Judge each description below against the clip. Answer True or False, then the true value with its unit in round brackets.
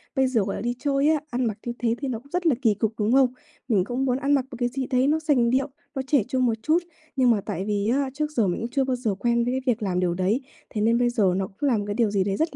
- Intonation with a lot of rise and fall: False (4.2 semitones)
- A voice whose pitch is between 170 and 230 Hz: False (245 Hz)